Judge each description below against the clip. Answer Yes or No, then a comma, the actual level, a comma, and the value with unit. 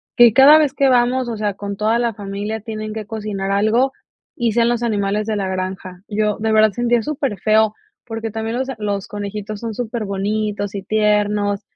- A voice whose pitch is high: Yes, high, 215 Hz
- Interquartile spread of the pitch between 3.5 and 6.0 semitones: No, narrow, 2.4 semitones